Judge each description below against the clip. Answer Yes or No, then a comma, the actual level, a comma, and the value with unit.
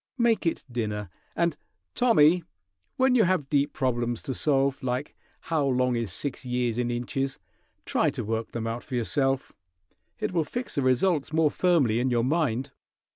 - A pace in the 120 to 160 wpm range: No, average, 170 wpm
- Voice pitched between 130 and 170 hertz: Yes, low, 135 Hz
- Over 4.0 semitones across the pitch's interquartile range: Yes, average, 4.7 semitones